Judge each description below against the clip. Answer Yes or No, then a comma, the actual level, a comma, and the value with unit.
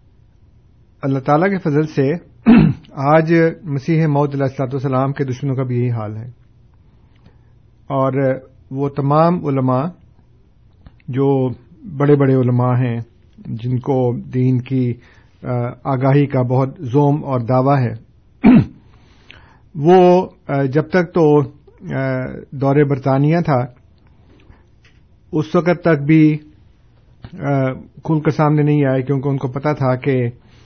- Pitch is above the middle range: No, low, 130 Hz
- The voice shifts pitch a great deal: No, average, 3.6 semitones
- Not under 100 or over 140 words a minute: Yes, average, 115 wpm